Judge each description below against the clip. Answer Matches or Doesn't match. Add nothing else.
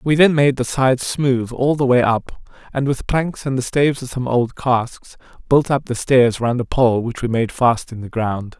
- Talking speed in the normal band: Doesn't match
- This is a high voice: Doesn't match